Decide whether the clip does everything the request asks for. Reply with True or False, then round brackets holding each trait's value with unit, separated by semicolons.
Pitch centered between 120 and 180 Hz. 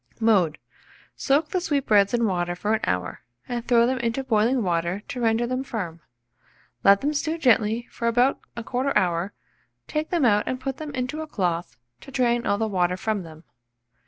False (230 Hz)